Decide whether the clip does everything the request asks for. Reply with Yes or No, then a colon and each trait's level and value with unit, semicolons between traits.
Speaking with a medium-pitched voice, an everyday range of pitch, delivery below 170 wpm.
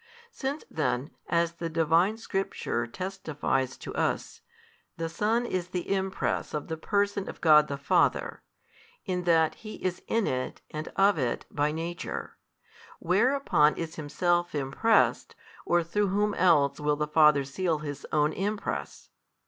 Yes: medium, 170 Hz; average, 4.4 semitones; average, 145 wpm